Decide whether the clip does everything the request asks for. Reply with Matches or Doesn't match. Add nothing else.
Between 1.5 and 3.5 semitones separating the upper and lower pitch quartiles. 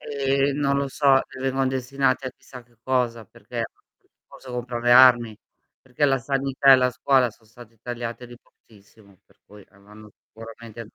Matches